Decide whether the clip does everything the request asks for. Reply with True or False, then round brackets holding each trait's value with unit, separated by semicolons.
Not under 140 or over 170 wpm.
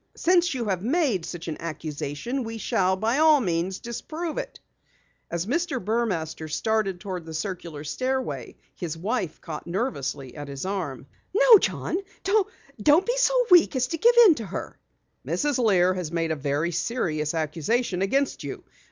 True (160 wpm)